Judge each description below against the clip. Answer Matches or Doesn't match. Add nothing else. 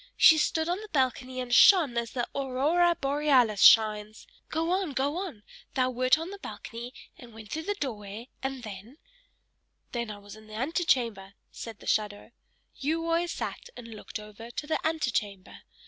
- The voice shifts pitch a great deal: Matches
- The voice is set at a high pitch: Matches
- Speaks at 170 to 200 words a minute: Matches